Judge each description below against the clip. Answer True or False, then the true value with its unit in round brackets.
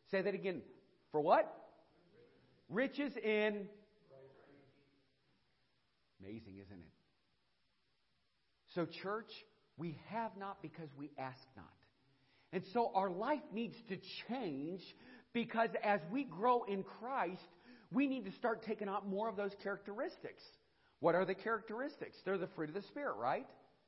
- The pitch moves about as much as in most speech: False (6.3 semitones)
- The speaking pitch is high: True (200 Hz)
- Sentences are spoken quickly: False (135 wpm)